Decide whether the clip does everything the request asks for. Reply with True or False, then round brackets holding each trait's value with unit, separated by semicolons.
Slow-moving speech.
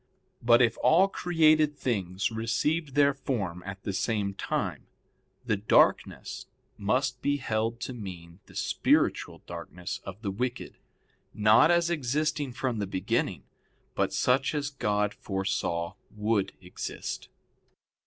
True (125 wpm)